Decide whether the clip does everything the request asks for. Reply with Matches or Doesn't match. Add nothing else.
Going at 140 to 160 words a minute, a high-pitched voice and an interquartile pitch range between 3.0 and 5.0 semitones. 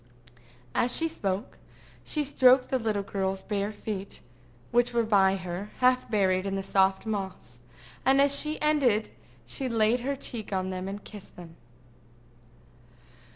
Matches